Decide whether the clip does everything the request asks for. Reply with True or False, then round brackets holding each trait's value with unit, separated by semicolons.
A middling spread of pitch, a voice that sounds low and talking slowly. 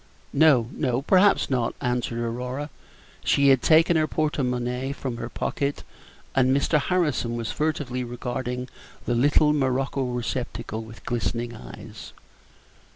True (3.1 semitones; 130 Hz; 130 wpm)